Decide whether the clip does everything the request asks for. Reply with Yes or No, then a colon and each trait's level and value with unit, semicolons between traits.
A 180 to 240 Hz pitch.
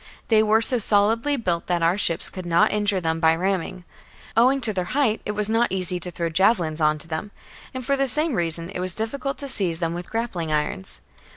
Yes: high, 190 Hz